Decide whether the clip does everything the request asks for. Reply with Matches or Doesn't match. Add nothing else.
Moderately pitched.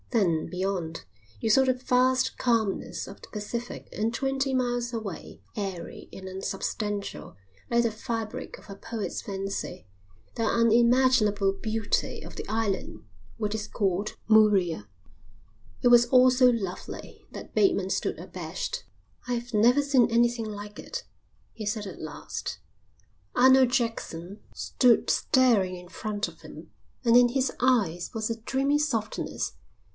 Doesn't match